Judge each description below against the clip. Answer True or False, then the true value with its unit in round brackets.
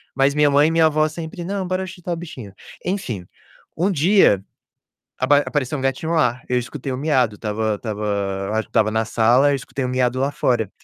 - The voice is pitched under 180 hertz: True (135 Hz)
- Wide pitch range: True (6.0 semitones)